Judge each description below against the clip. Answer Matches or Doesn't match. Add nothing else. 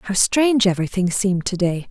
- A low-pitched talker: Doesn't match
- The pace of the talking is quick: Doesn't match